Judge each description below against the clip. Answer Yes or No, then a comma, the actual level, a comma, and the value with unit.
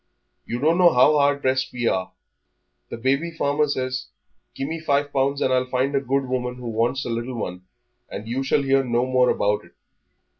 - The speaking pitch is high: No, low, 130 Hz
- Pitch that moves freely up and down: No, narrow, 2.4 semitones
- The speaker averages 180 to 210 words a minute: Yes, average, 200 wpm